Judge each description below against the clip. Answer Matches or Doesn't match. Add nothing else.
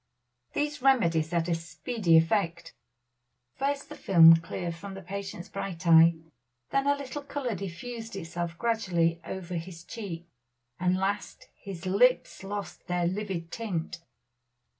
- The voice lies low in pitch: Doesn't match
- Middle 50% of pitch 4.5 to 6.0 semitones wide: Matches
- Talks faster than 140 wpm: Doesn't match